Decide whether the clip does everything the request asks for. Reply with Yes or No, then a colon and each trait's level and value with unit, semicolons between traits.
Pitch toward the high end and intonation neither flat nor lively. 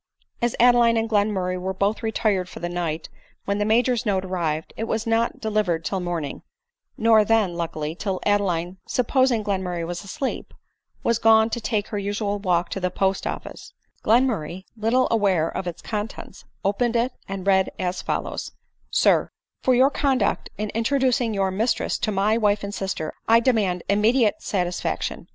Yes: high, 205 Hz; average, 3.6 semitones